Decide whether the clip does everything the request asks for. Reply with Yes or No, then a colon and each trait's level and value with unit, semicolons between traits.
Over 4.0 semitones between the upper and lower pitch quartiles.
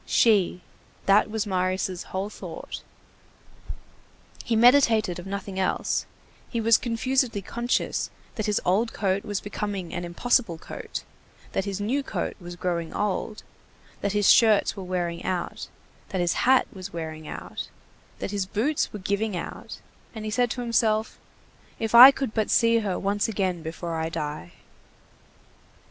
No: average, 3.6 semitones